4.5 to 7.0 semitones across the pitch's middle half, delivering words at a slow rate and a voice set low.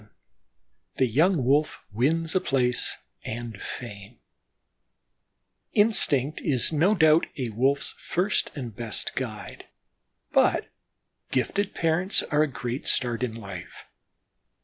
Yes: average, 5.3 semitones; slow, 115 wpm; low, 130 Hz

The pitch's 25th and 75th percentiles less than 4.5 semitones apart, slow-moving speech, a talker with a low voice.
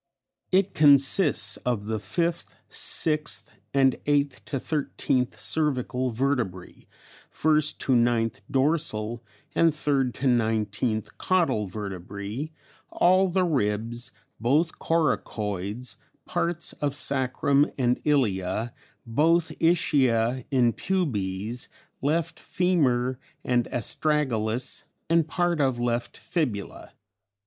No: average, 5.2 semitones; slow, 100 wpm; low, 130 Hz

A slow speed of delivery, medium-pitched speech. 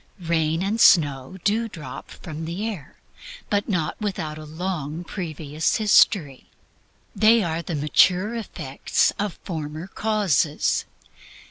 Yes: slow, 120 wpm; medium, 170 Hz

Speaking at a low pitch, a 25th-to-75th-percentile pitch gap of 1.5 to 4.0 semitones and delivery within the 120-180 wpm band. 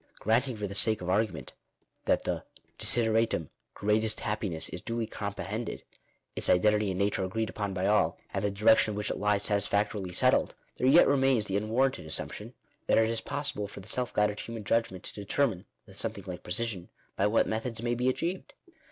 No: low, 105 Hz; narrow, 2.4 semitones; average, 195 wpm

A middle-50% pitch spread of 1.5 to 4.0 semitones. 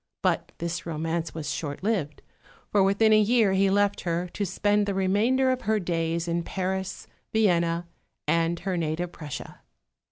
Yes: average, 3.4 semitones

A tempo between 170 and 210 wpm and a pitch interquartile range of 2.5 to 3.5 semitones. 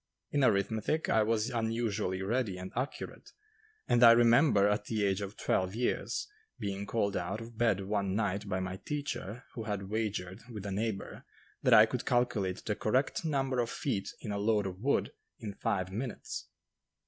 Yes: average, 175 wpm; average, 3.2 semitones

